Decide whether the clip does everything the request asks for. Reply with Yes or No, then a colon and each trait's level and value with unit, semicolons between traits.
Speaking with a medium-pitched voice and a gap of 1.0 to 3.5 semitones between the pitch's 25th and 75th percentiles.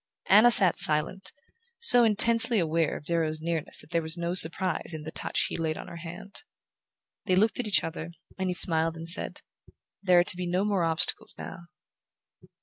Yes: medium, 175 Hz; average, 3.1 semitones